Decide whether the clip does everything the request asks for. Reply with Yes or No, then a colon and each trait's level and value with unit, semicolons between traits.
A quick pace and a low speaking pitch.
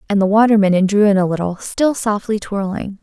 No: fast, 220 wpm; high, 205 Hz